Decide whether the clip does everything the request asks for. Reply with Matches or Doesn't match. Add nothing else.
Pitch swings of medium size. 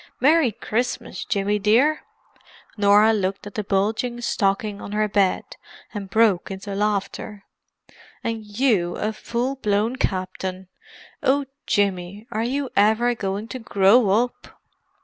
Matches